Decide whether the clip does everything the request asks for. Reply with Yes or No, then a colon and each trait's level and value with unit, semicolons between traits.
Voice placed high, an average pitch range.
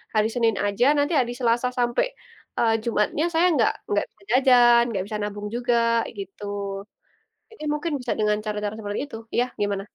Yes: high, 230 Hz; average, 3.0 semitones